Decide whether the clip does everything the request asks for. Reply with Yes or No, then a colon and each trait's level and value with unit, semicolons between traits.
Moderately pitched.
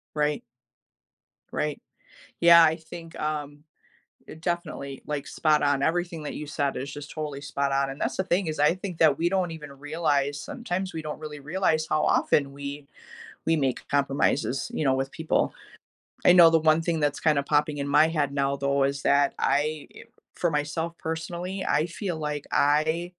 Yes: medium, 150 Hz